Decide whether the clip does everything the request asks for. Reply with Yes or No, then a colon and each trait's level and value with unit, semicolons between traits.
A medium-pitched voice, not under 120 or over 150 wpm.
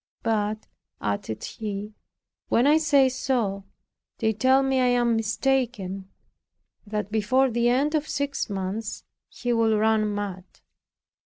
No: high, 225 Hz; slow, 135 wpm